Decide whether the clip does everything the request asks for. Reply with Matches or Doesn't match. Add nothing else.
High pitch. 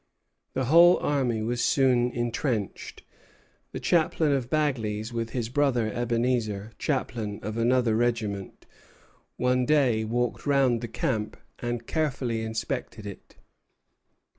Doesn't match